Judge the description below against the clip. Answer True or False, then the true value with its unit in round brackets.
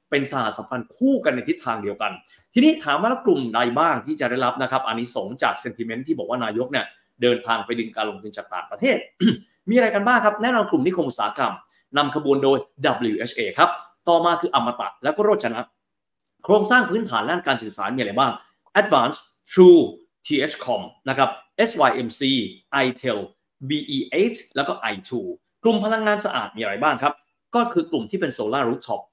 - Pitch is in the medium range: True (155 Hz)